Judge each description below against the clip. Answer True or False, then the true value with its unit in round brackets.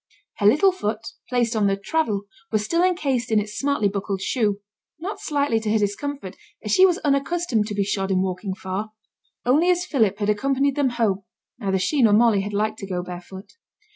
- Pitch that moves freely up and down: True (5.7 semitones)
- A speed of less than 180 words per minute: False (200 wpm)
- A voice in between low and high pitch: False (220 Hz)